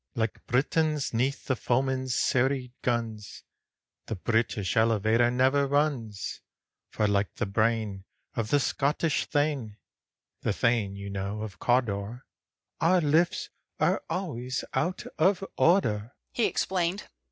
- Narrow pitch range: No, average, 4.9 semitones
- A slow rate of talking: Yes, slow, 120 wpm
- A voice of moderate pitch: No, low, 120 Hz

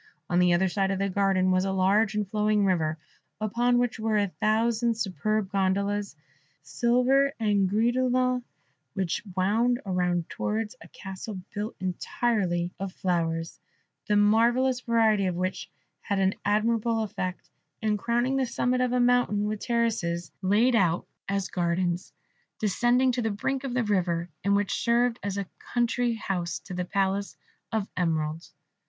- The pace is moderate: Yes, average, 160 wpm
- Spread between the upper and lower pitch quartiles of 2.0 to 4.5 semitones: Yes, average, 4.0 semitones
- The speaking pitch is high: Yes, high, 205 Hz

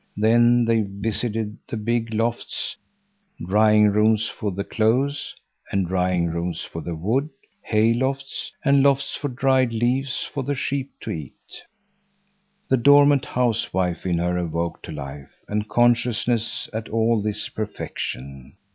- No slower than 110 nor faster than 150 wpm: Yes, average, 140 wpm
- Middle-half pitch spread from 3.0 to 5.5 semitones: Yes, average, 4.8 semitones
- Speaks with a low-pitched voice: Yes, low, 110 Hz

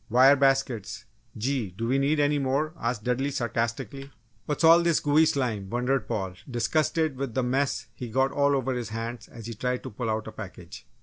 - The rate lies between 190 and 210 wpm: Yes, average, 195 wpm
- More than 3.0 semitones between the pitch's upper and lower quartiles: Yes, average, 3.4 semitones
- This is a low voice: Yes, low, 130 Hz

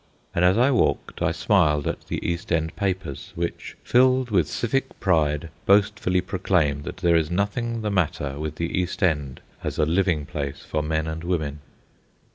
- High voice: No, very low, 85 Hz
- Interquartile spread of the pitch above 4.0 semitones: Yes, average, 4.5 semitones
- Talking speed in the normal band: Yes, average, 175 wpm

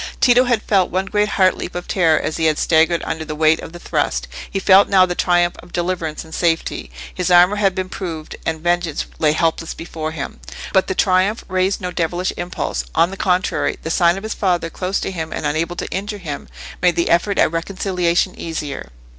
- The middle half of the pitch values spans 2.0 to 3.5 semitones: Yes, narrow, 2.6 semitones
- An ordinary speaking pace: No, fast, 215 wpm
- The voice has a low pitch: No, medium, 175 Hz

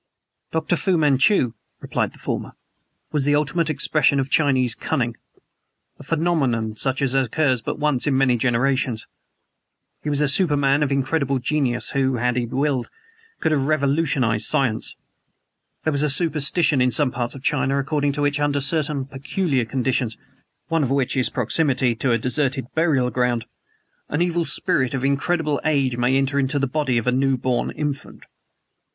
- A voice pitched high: No, low, 135 Hz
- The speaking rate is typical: Yes, average, 165 wpm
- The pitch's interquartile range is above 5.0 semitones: No, average, 2.8 semitones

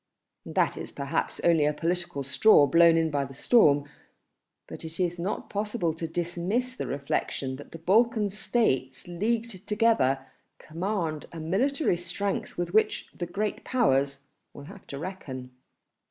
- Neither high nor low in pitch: Yes, medium, 170 Hz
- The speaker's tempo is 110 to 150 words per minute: Yes, average, 145 wpm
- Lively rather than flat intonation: Yes, wide, 6.2 semitones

